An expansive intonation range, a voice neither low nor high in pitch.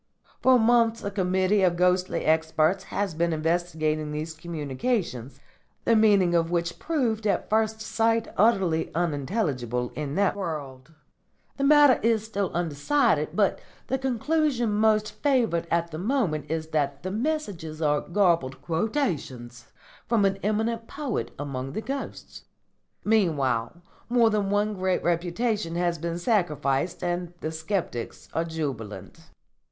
Yes: wide, 5.8 semitones; medium, 180 Hz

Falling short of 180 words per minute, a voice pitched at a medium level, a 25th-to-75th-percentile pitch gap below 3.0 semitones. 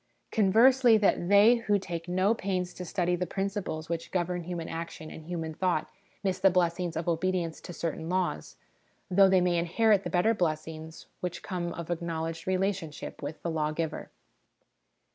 Yes: average, 165 wpm; medium, 175 Hz; narrow, 2.5 semitones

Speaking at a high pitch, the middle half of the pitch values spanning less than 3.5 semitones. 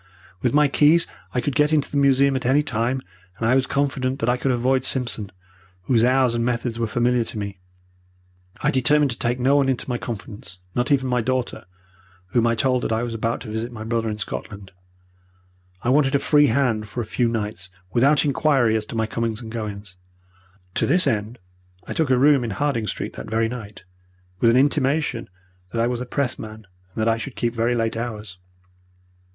No: low, 120 Hz; average, 3.0 semitones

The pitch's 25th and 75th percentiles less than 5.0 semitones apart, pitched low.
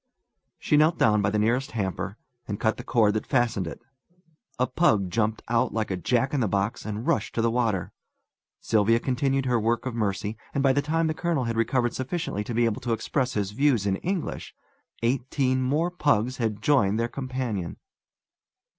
Yes: average, 3.8 semitones; low, 115 Hz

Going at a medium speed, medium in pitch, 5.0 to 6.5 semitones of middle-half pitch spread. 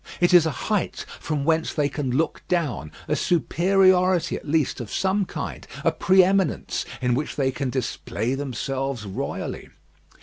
Yes: average, 160 wpm; medium, 155 Hz; average, 5.3 semitones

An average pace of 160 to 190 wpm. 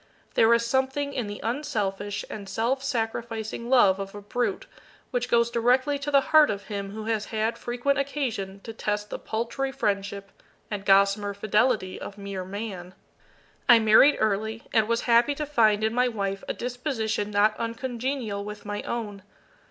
Yes: average, 165 wpm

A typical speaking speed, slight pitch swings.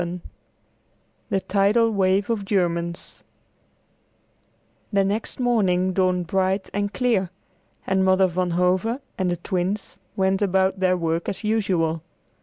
No: slow, 125 wpm; narrow, 2.0 semitones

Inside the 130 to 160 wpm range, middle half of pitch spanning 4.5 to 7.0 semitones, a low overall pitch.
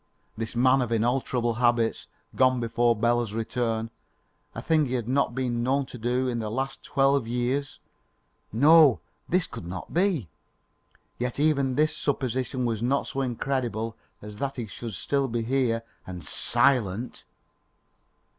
No: average, 150 wpm; average, 2.9 semitones; low, 125 Hz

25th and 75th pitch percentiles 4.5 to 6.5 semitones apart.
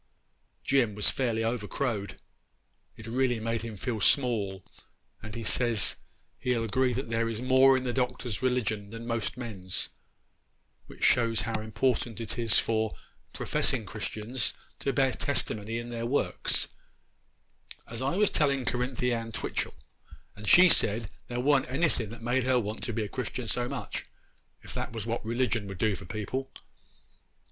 No: average, 2.7 semitones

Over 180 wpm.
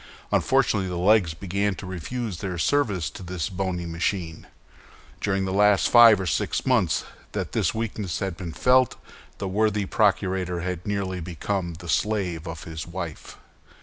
No: average, 155 wpm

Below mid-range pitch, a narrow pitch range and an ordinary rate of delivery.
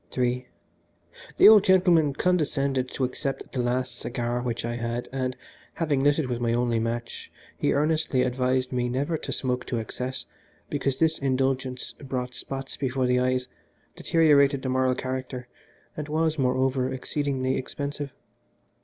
Yes: low, 130 Hz; narrow, 2.1 semitones; average, 150 wpm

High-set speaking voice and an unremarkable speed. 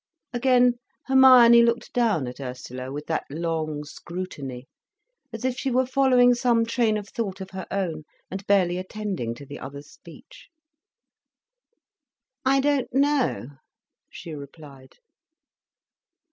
No: high, 195 Hz; slow, 125 wpm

